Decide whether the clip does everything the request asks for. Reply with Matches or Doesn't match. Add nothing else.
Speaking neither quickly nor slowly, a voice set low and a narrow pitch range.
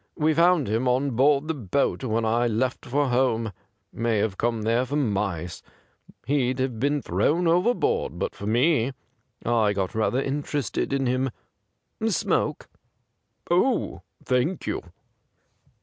Doesn't match